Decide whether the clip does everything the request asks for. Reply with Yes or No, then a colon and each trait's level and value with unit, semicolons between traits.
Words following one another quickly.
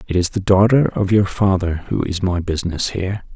Yes: fast, 215 wpm